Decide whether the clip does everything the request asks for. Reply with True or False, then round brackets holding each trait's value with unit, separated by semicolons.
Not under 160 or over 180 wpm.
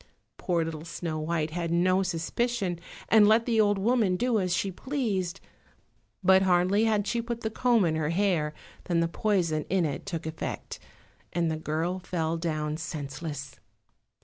True (165 wpm)